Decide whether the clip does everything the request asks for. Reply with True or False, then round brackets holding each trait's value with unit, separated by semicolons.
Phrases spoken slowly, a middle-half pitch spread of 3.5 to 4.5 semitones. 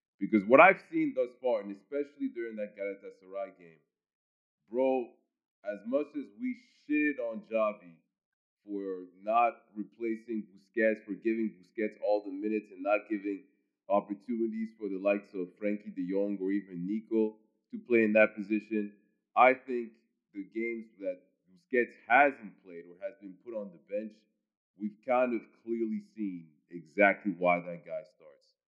False (155 wpm; 4.0 semitones)